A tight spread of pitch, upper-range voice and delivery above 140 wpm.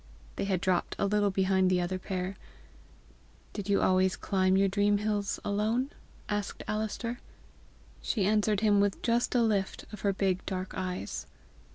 Yes: narrow, 2.0 semitones; high, 200 Hz; average, 160 wpm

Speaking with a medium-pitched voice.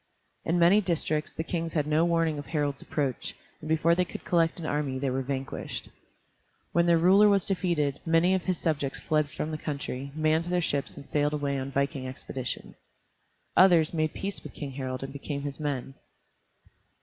Yes: medium, 155 Hz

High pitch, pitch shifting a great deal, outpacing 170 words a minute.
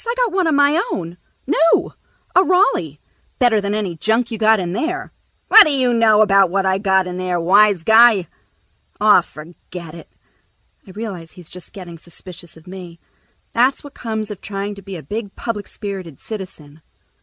No: high, 200 Hz; average, 4.3 semitones; average, 180 wpm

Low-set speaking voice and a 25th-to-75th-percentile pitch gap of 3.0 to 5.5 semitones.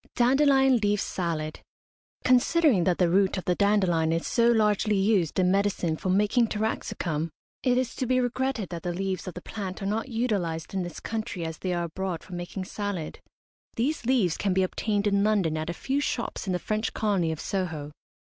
No: high, 195 Hz; average, 4.3 semitones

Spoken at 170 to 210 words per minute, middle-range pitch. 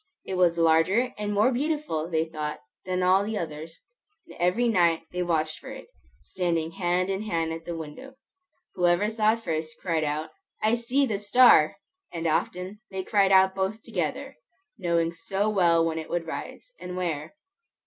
Yes: average, 175 wpm; medium, 180 Hz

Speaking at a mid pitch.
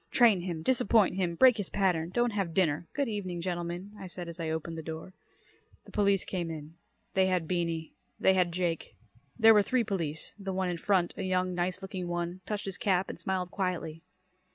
Yes: medium, 180 Hz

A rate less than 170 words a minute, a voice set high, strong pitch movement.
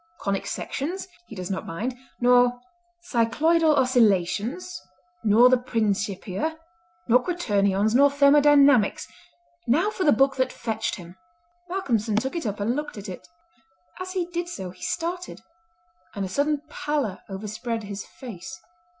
Yes: average, 140 wpm; high, 245 Hz; wide, 6.4 semitones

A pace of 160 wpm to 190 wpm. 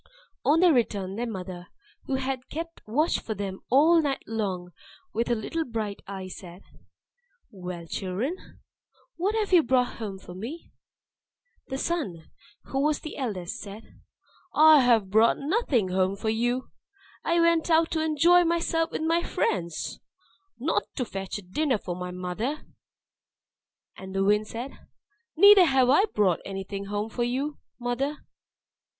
No: average, 145 wpm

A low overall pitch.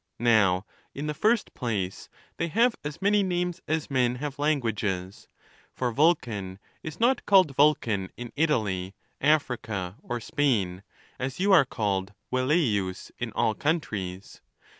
Yes: low, 125 Hz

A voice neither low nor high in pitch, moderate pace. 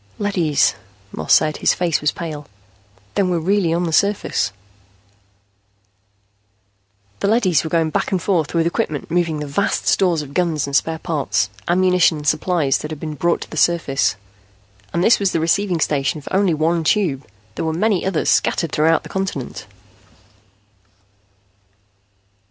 Yes: medium, 165 Hz; average, 155 wpm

